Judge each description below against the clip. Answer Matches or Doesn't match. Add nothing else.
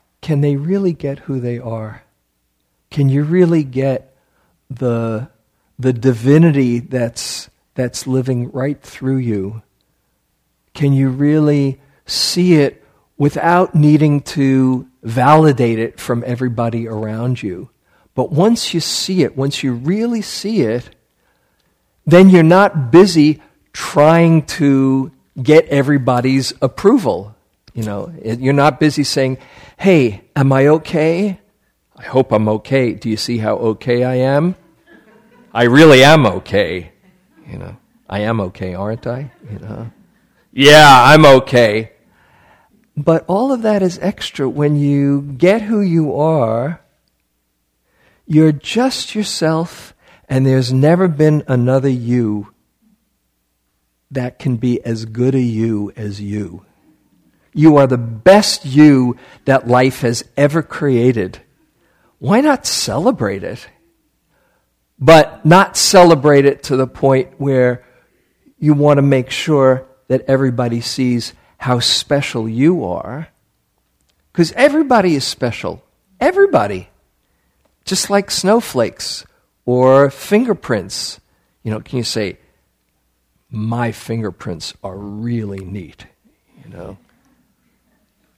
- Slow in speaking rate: Matches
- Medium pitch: Doesn't match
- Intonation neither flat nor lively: Matches